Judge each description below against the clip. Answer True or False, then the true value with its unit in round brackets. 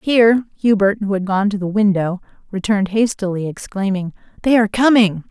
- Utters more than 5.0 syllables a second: True (5.6 syllables/s)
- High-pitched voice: True (205 Hz)